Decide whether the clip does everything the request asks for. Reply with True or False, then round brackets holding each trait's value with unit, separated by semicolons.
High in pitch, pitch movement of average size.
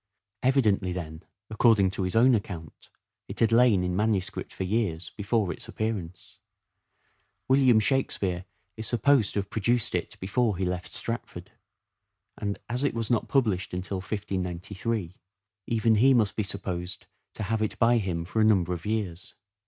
False (105 Hz; 3.9 semitones)